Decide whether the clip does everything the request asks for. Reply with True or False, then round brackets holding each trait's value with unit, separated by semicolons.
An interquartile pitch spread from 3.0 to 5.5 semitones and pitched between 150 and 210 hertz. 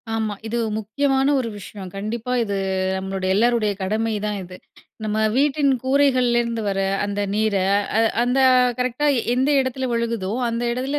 False (3.7 semitones; 230 Hz)